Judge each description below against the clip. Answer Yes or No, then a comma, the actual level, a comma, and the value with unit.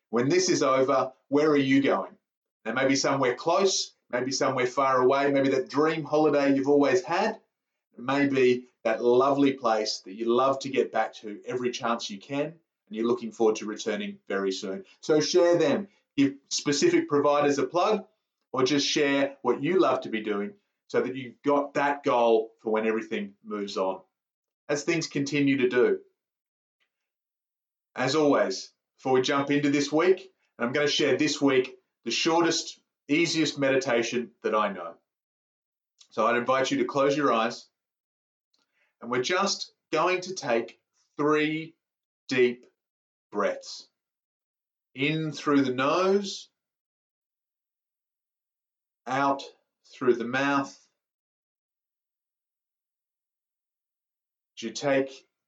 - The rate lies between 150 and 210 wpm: No, average, 140 wpm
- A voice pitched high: No, medium, 140 Hz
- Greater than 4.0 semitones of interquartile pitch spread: Yes, average, 4.8 semitones